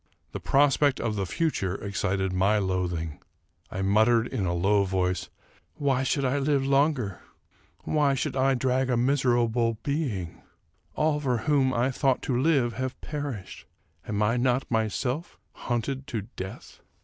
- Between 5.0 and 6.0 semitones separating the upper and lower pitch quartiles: Yes, average, 5.3 semitones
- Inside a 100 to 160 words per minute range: Yes, average, 155 wpm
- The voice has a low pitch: Yes, low, 120 Hz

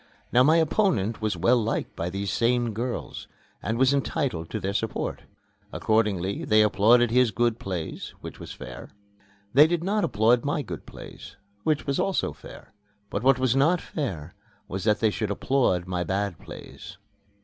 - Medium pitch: No, low, 115 Hz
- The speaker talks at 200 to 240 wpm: No, average, 170 wpm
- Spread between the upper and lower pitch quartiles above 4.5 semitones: Yes, average, 5.1 semitones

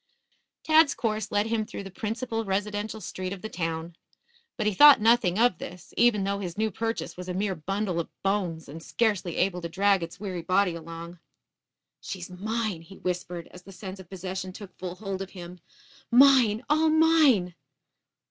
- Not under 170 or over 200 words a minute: Yes, average, 180 wpm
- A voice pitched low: No, high, 195 Hz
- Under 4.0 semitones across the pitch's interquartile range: Yes, average, 3.5 semitones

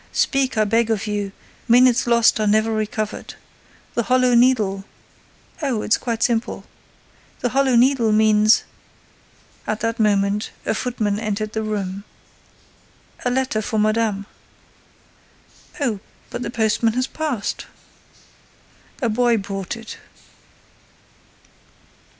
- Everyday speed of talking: No, slow, 115 wpm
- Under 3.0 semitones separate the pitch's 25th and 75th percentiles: Yes, narrow, 2.4 semitones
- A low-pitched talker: No, high, 220 Hz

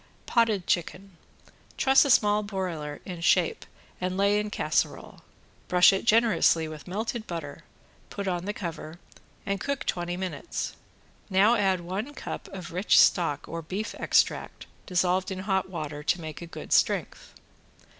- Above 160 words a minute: No, average, 150 wpm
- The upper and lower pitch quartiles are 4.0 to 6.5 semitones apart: No, average, 3.2 semitones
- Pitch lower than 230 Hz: Yes, medium, 185 Hz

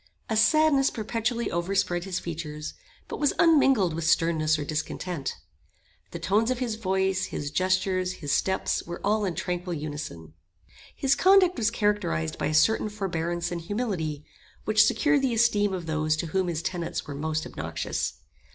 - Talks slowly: No, average, 160 wpm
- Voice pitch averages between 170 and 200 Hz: Yes, medium, 185 Hz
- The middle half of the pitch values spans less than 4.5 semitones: No, wide, 5.4 semitones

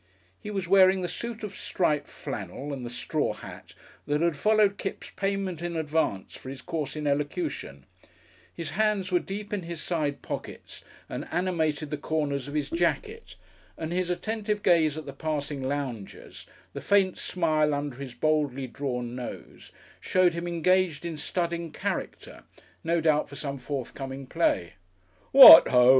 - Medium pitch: Yes, medium, 160 Hz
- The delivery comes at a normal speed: Yes, average, 160 wpm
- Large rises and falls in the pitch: No, average, 4.4 semitones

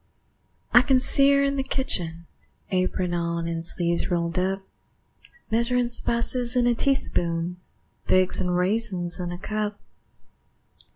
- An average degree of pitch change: No, wide, 5.7 semitones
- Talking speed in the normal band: No, slow, 130 wpm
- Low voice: No, medium, 185 Hz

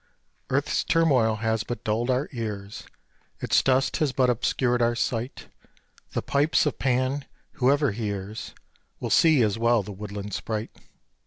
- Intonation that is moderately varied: Yes, average, 3.5 semitones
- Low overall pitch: Yes, low, 120 Hz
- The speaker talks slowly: No, average, 145 wpm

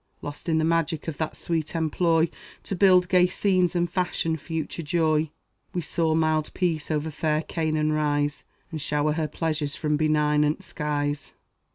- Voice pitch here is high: No, medium, 155 Hz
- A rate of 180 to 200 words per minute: No, average, 160 wpm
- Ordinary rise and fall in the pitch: No, narrow, 1.8 semitones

